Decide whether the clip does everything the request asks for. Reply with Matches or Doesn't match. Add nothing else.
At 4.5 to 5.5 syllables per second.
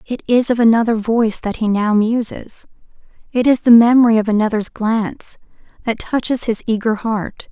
Matches